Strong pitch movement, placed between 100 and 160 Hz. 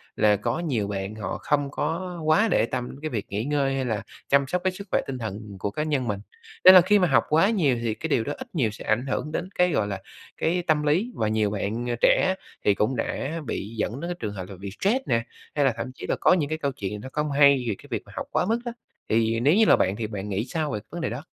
Yes: wide, 6.6 semitones; low, 135 Hz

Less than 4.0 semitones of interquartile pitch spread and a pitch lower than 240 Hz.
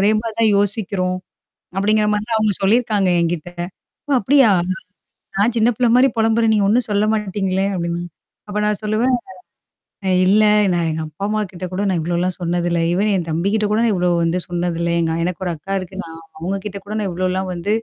Yes: average, 3.4 semitones; high, 195 Hz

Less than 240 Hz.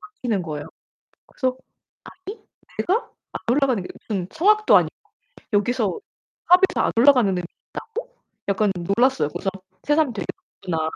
No: very high, 250 Hz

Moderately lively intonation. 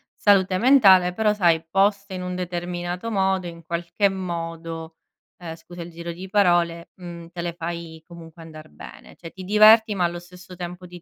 No: narrow, 2.1 semitones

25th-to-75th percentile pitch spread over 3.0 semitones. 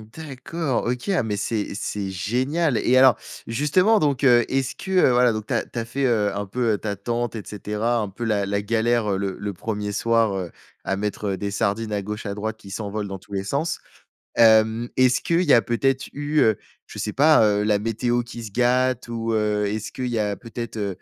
Yes: average, 3.4 semitones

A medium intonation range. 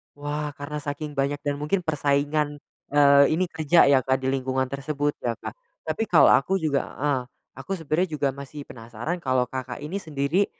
No: narrow, 2.1 semitones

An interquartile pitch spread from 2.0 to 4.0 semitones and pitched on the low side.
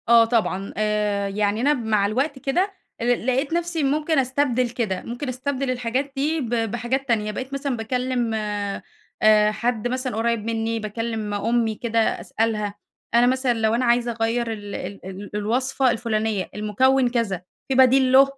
No: average, 3.3 semitones; high, 235 Hz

